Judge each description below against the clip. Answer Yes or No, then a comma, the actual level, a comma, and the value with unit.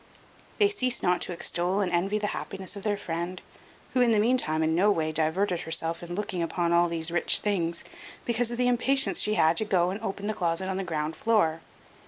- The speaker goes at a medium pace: No, fast, 220 wpm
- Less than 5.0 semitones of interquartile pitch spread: Yes, average, 4.0 semitones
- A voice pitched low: No, medium, 185 Hz